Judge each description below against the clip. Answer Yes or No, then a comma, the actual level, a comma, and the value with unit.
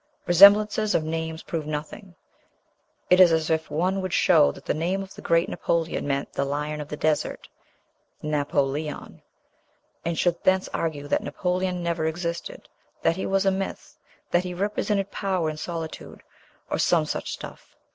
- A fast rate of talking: No, average, 165 wpm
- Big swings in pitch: No, average, 3.2 semitones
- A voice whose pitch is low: No, medium, 170 Hz